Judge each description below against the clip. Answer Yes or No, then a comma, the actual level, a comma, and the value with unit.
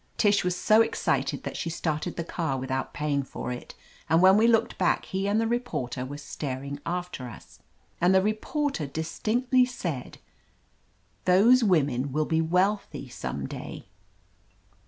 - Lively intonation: Yes, wide, 6.9 semitones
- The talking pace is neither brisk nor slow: Yes, average, 155 wpm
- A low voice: No, medium, 170 Hz